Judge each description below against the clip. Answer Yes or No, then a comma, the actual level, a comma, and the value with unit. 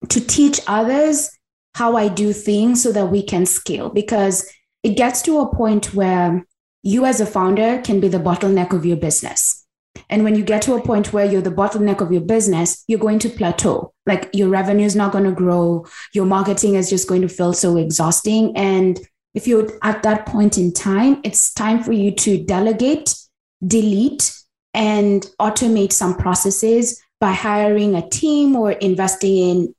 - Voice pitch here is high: Yes, high, 205 Hz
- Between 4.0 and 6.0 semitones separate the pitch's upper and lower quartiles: No, average, 2.8 semitones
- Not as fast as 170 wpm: No, average, 185 wpm